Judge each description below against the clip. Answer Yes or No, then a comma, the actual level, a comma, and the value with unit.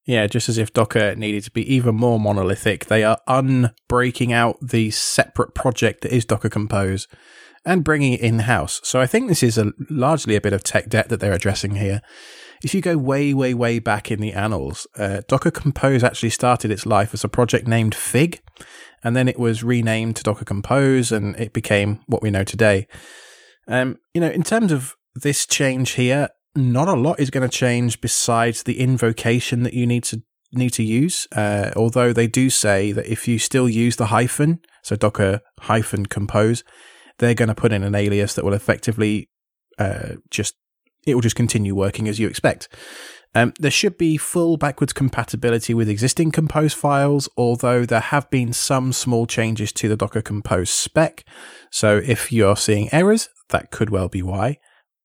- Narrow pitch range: No, average, 3.3 semitones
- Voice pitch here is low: Yes, low, 115 Hz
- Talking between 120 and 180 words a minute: No, average, 190 wpm